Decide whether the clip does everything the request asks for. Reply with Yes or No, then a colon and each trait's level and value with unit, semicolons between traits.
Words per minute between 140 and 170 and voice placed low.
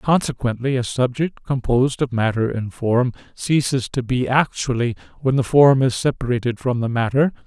Yes: average, 160 wpm; low, 125 Hz